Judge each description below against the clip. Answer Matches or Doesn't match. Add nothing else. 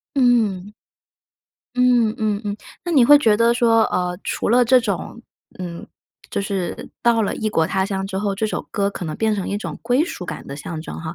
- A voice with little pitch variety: Doesn't match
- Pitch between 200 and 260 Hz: Matches